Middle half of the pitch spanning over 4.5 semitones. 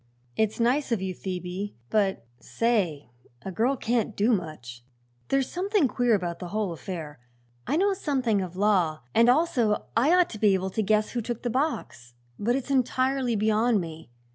Yes: average, 5.2 semitones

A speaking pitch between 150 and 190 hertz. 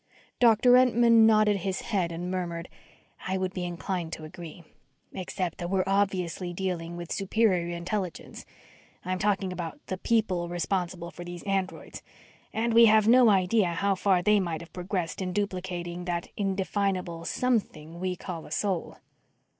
Yes: medium, 185 Hz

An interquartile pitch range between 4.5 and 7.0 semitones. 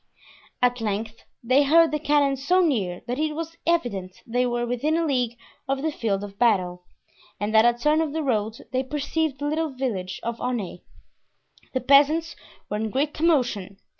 Yes: wide, 5.4 semitones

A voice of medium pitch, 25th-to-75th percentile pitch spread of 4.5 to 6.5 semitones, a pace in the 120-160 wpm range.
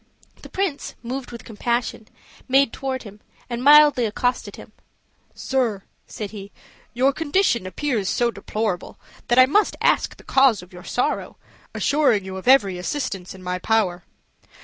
No: high, 235 Hz; average, 5.2 semitones; average, 150 wpm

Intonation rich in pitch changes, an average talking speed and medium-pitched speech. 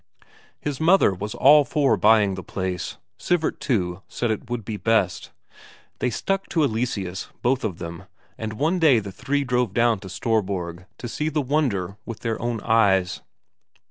No: wide, 5.7 semitones; average, 170 wpm; low, 115 Hz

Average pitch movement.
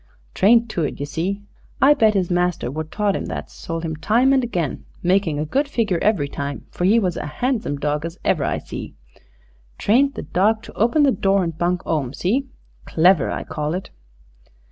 No: wide, 5.9 semitones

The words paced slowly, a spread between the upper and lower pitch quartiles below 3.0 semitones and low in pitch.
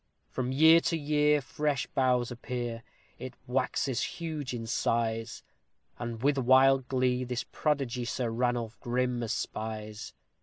Yes: slow, 125 wpm; narrow, 2.5 semitones; low, 125 Hz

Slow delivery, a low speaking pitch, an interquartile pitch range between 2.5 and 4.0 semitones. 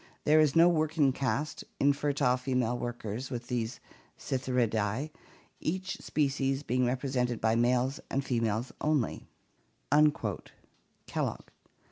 Yes: slow, 110 wpm; low, 130 Hz; average, 2.9 semitones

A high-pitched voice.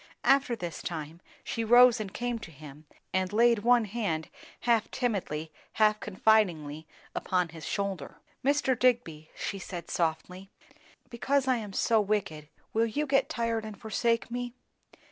Yes: high, 215 Hz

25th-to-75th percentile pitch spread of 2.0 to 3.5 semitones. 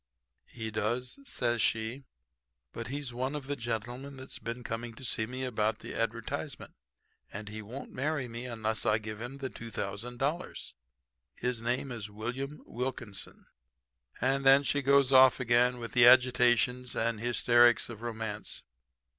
Yes: narrow, 2.6 semitones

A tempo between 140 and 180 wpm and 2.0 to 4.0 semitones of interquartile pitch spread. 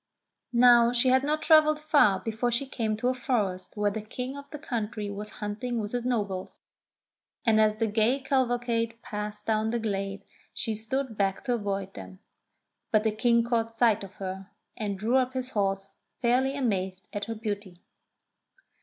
Yes: average, 175 wpm; average, 3.3 semitones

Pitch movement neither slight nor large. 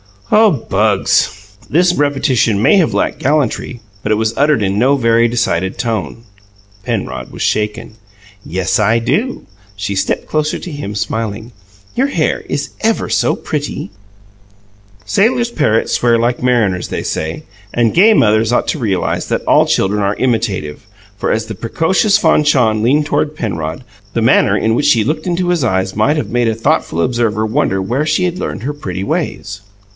No: wide, 6.1 semitones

